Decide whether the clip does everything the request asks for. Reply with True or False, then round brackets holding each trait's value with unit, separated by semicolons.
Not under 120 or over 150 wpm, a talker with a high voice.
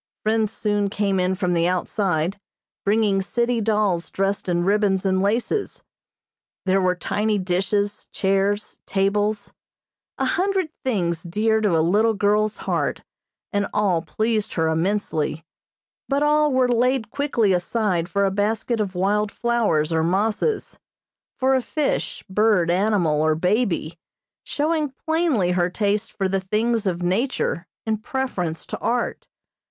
True (140 wpm; 205 Hz)